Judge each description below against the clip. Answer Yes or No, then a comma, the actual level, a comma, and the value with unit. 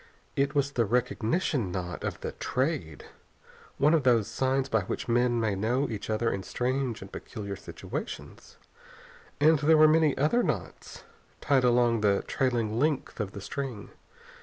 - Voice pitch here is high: No, low, 125 Hz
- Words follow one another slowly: No, average, 160 wpm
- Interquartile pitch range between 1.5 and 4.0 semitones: No, average, 4.5 semitones